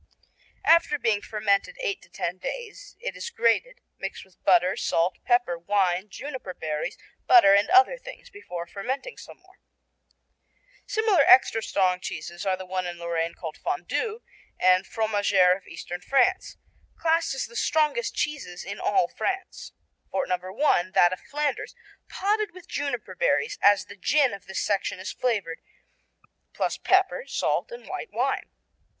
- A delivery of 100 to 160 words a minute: Yes, average, 155 wpm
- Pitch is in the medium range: No, high, 225 Hz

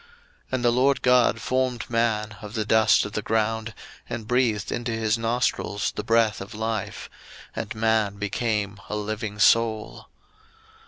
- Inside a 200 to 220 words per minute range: No, average, 155 wpm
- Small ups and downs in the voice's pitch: Yes, narrow, 1.8 semitones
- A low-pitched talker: Yes, low, 110 Hz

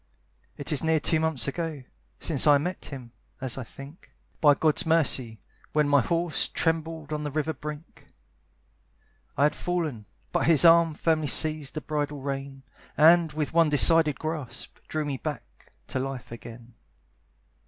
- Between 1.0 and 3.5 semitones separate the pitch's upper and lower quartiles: Yes, average, 2.8 semitones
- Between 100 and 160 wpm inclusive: Yes, average, 155 wpm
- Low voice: No, medium, 150 Hz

